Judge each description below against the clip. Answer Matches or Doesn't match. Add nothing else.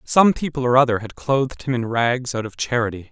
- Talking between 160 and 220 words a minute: Doesn't match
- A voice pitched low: Matches